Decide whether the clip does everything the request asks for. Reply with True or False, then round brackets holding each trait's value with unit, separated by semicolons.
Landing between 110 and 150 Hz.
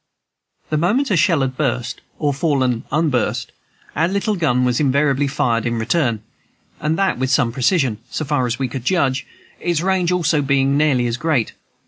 True (140 Hz)